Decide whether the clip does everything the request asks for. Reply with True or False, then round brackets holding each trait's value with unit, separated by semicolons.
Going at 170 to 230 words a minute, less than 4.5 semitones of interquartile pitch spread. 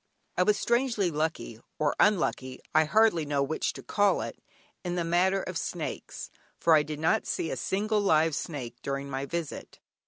False (180 wpm; 4.8 semitones)